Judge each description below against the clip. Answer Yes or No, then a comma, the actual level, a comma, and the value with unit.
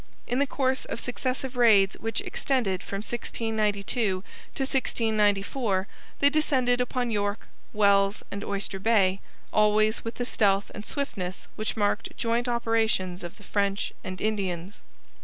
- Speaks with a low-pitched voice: No, high, 215 Hz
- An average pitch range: Yes, average, 3.4 semitones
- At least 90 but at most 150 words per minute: Yes, average, 140 wpm